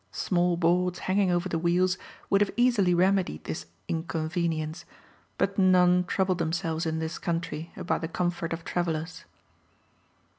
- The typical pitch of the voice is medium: Yes, medium, 175 Hz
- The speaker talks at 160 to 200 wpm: No, average, 140 wpm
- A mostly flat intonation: Yes, narrow, 1.9 semitones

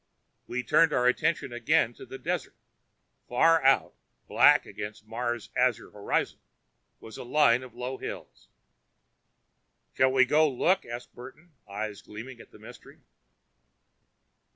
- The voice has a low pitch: Yes, low, 125 Hz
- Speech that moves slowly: Yes, slow, 130 wpm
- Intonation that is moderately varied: No, narrow, 2.2 semitones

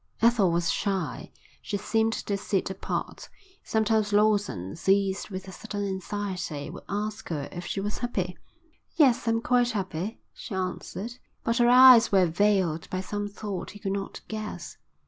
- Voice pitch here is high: Yes, high, 205 Hz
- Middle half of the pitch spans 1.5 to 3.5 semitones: Yes, average, 2.8 semitones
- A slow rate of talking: No, average, 160 wpm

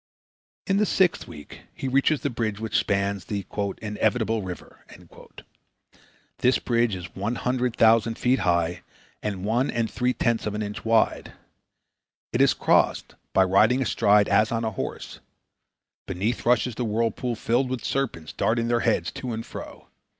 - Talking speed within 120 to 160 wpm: Yes, average, 155 wpm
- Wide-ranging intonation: No, average, 3.3 semitones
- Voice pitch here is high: No, low, 115 Hz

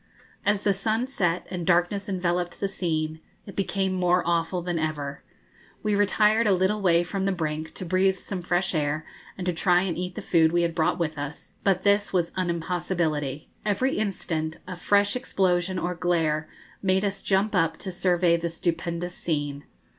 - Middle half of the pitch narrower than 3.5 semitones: Yes, average, 2.7 semitones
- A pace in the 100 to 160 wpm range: No, average, 185 wpm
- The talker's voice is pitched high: No, medium, 180 Hz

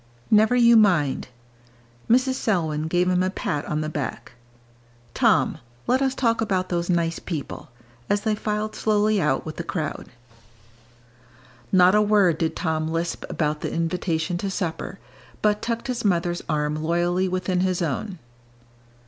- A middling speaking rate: Yes, average, 150 wpm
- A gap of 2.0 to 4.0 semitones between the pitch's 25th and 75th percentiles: No, average, 4.5 semitones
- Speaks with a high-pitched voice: No, medium, 180 Hz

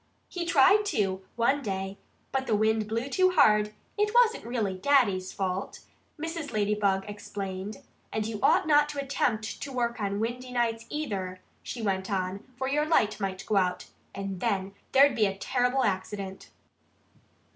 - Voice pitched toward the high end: Yes, high, 215 Hz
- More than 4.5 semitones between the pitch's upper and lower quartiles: Yes, wide, 5.5 semitones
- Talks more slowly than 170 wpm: Yes, average, 160 wpm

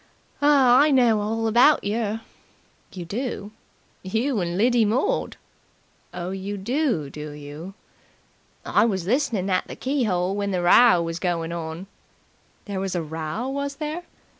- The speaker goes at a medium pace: Yes, average, 145 wpm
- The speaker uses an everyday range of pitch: No, wide, 6.1 semitones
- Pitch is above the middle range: Yes, high, 205 Hz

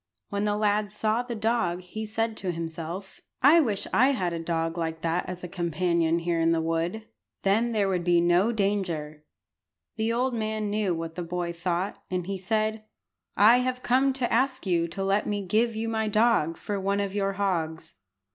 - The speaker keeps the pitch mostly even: No, average, 4.3 semitones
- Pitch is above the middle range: Yes, high, 195 Hz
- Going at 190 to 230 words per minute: Yes, average, 195 wpm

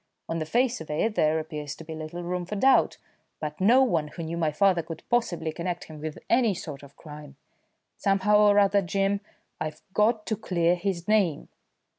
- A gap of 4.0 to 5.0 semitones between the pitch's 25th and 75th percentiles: Yes, average, 4.5 semitones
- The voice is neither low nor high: Yes, medium, 175 Hz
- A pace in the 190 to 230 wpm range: Yes, average, 195 wpm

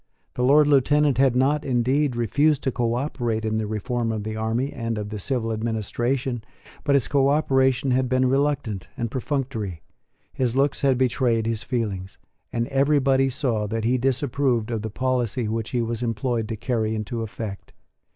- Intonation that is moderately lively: Yes, average, 3.2 semitones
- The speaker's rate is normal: Yes, average, 170 wpm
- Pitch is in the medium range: No, low, 120 Hz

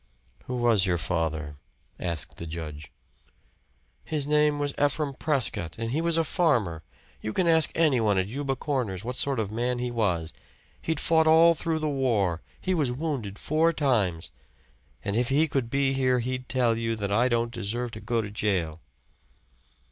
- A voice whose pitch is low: Yes, low, 120 Hz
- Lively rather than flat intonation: Yes, wide, 6.2 semitones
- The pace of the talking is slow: No, average, 180 wpm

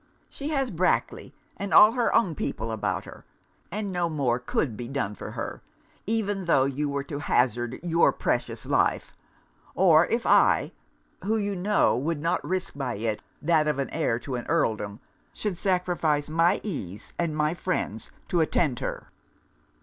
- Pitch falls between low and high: Yes, medium, 160 Hz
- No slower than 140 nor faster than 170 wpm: Yes, average, 165 wpm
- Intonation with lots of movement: Yes, wide, 6.0 semitones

